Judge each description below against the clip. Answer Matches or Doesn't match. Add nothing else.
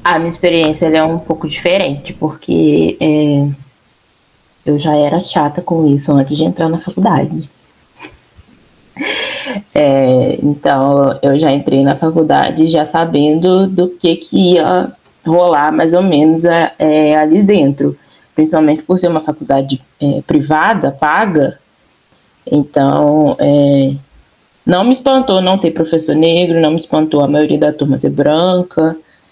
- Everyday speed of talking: Matches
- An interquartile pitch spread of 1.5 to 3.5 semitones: Matches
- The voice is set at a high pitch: Doesn't match